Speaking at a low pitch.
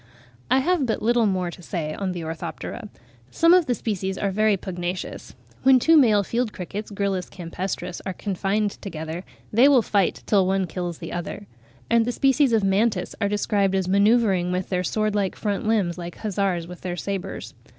No: high, 195 Hz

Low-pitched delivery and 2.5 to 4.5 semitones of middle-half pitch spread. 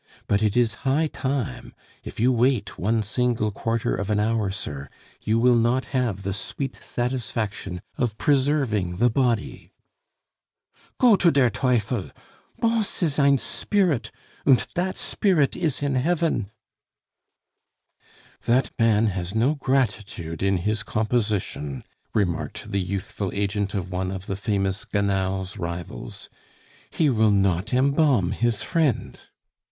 No: low, 110 Hz; average, 5.1 semitones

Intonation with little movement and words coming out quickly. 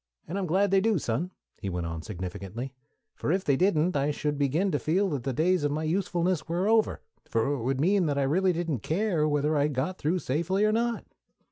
No: average, 5.1 semitones; fast, 225 wpm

